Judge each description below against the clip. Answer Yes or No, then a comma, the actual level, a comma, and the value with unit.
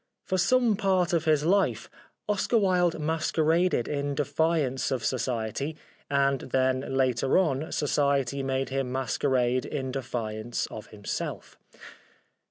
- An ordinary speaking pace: No, slow, 120 wpm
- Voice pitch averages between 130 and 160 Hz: Yes, medium, 140 Hz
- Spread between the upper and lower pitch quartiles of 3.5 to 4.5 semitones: Yes, average, 4.0 semitones